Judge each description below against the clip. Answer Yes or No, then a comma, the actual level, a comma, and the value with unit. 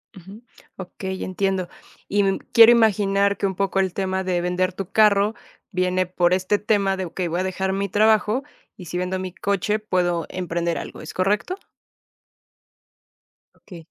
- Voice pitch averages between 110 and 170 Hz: No, high, 190 Hz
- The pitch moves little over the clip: Yes, narrow, 1.7 semitones